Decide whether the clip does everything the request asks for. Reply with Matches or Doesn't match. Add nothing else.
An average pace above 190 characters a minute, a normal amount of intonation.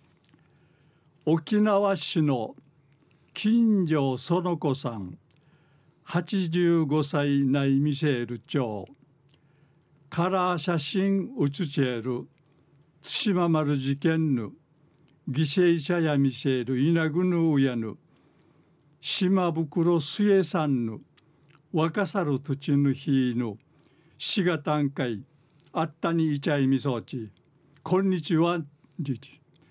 Doesn't match